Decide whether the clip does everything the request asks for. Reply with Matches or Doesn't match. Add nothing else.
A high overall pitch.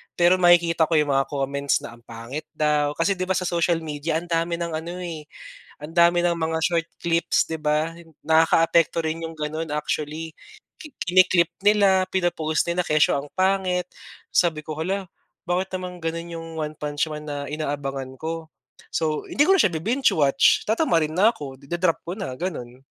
Doesn't match